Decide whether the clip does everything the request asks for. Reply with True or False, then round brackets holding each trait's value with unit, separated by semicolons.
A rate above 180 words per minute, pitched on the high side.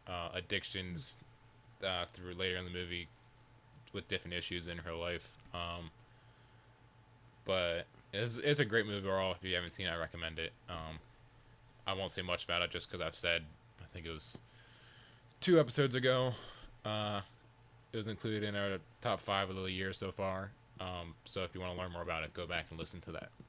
False (195 wpm; 100 Hz)